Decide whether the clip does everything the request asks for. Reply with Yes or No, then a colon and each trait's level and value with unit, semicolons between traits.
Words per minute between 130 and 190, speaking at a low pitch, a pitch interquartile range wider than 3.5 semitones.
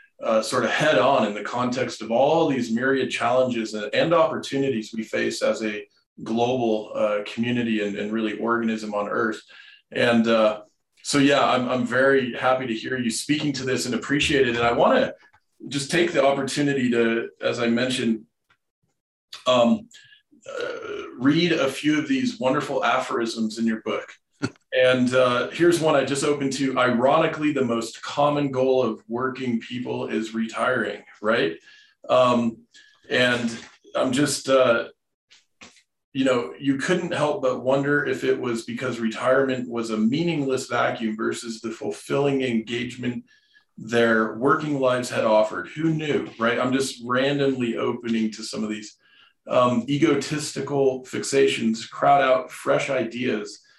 Yes: average, 150 wpm; low, 130 Hz; average, 4.0 semitones